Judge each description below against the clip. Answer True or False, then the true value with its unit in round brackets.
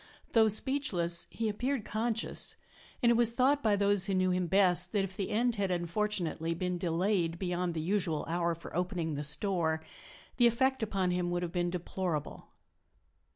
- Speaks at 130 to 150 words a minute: False (175 wpm)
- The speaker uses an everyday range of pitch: True (3.9 semitones)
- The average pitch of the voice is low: False (185 Hz)